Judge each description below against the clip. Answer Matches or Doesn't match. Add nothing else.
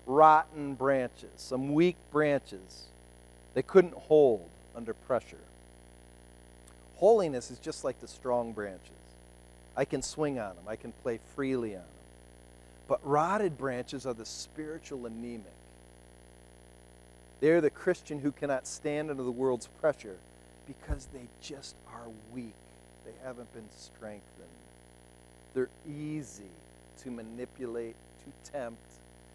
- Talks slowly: Matches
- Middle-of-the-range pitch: Doesn't match